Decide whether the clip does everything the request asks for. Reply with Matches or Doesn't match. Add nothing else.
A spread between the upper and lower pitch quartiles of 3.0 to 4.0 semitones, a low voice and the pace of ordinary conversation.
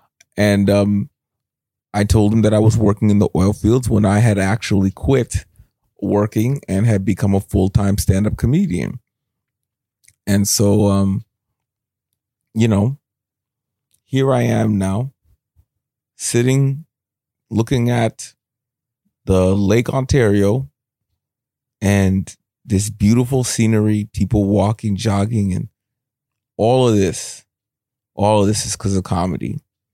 Doesn't match